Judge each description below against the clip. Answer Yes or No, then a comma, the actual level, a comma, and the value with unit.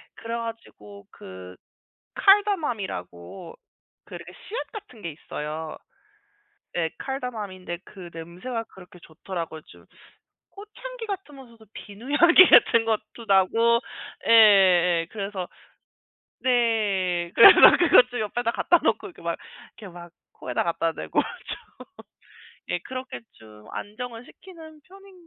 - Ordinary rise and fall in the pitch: No, wide, 6.8 semitones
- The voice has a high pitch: Yes, high, 215 Hz